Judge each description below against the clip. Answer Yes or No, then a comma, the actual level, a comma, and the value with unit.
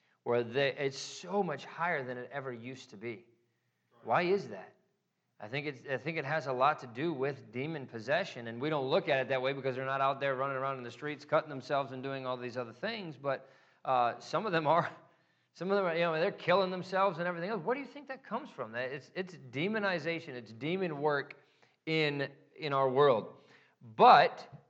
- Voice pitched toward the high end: No, medium, 140 Hz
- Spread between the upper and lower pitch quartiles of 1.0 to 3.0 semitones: No, average, 4.3 semitones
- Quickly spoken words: Yes, fast, 220 wpm